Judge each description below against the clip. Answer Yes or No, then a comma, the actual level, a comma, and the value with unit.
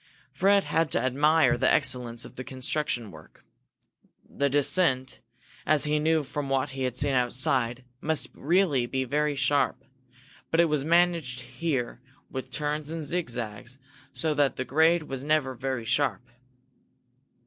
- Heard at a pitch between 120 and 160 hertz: Yes, medium, 140 Hz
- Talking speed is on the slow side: No, average, 150 wpm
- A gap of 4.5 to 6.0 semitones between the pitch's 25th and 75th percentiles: No, average, 3.3 semitones